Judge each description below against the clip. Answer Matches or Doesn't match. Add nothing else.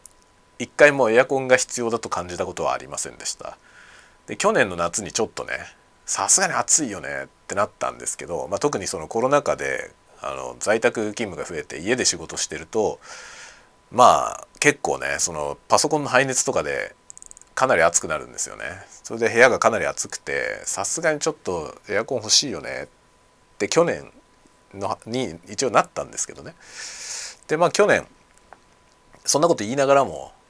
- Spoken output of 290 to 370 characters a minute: Matches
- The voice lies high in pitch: Doesn't match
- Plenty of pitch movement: Doesn't match